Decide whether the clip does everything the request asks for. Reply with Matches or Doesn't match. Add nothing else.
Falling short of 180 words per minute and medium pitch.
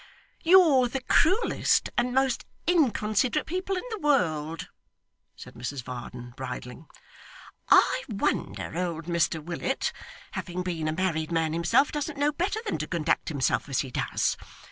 Matches